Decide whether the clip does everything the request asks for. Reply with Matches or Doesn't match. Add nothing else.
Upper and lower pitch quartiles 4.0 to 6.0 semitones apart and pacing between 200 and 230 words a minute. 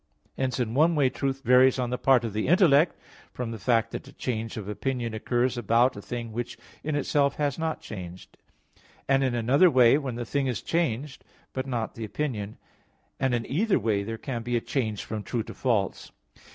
Doesn't match